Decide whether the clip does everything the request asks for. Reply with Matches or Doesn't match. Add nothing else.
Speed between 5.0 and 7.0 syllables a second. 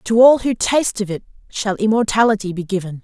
Matches